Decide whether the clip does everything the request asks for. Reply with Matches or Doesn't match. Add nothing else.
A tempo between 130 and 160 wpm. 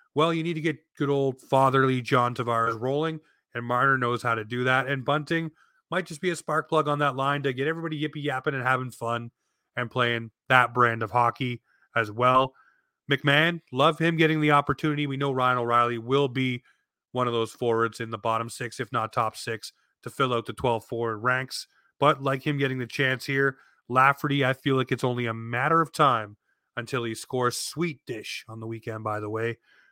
Doesn't match